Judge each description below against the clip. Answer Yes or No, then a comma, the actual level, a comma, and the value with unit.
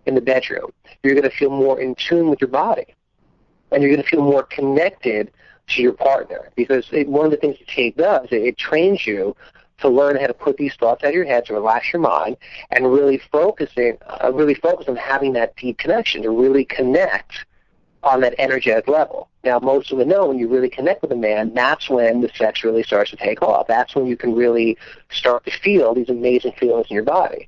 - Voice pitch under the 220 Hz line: Yes, low, 135 Hz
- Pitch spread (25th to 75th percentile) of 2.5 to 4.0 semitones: Yes, average, 2.9 semitones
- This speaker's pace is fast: Yes, fast, 225 wpm